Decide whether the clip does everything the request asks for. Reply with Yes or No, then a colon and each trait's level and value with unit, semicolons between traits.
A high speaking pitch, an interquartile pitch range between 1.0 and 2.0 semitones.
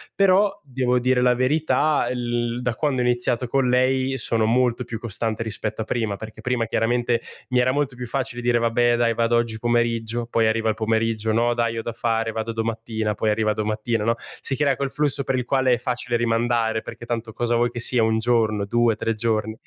No: low, 120 Hz; narrow, 1.7 semitones